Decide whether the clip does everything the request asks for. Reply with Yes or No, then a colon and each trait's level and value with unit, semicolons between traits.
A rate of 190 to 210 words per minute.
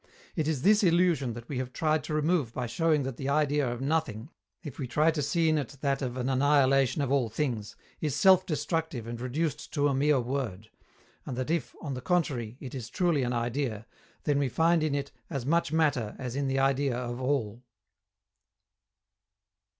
Yes: average, 195 wpm